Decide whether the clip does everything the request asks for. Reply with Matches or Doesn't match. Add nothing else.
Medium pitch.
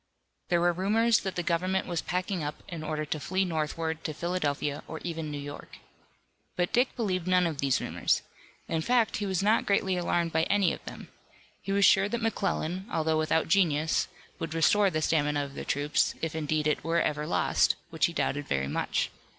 Matches